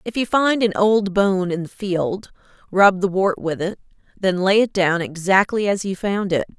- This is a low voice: No, high, 190 Hz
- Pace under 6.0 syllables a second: Yes, 4.5 syllables/s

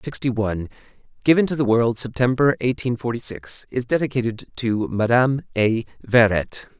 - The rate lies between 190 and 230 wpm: No, average, 140 wpm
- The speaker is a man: Yes, male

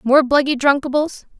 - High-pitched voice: Yes, very high, 275 Hz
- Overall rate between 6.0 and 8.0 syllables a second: No, 5.1 syllables/s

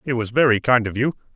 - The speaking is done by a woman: No, male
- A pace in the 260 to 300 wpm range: Yes, fast, 265 wpm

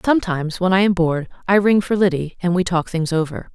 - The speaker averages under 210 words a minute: No, fast, 235 wpm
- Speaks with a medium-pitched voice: Yes, medium, 180 Hz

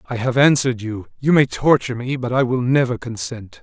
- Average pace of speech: No, fast, 215 wpm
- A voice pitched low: Yes, low, 125 Hz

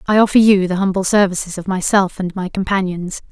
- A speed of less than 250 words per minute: Yes, average, 200 wpm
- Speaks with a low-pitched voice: No, high, 190 Hz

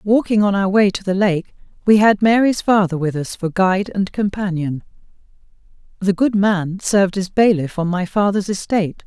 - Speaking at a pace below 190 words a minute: Yes, average, 180 wpm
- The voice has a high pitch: Yes, high, 195 Hz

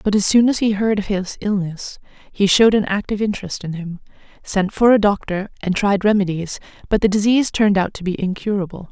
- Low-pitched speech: No, high, 200 Hz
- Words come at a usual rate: No, fast, 210 wpm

